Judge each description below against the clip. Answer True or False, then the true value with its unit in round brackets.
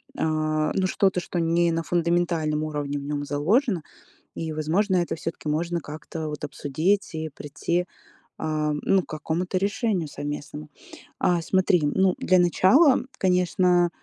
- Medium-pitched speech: True (165 Hz)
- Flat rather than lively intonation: False (3.0 semitones)